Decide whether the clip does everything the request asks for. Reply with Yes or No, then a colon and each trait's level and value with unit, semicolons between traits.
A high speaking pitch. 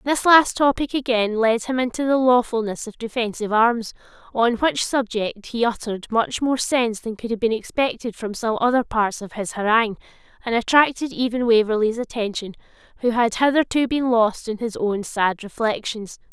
Yes: high, 230 Hz